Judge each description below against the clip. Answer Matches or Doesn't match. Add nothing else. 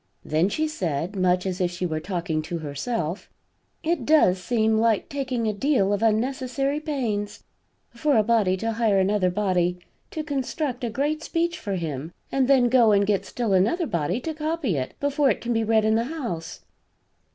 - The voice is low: Doesn't match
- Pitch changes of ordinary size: Doesn't match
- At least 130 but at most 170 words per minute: Doesn't match